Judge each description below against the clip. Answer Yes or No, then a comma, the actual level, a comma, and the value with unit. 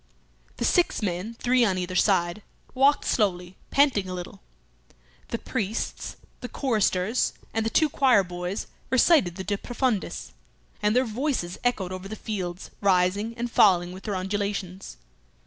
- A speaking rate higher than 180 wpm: No, average, 145 wpm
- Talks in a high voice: Yes, high, 205 Hz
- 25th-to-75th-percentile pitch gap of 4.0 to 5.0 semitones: Yes, average, 4.7 semitones